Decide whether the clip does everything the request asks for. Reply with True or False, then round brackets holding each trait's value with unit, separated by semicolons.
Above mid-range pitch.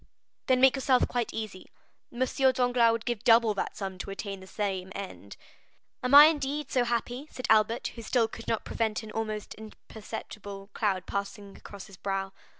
True (220 Hz)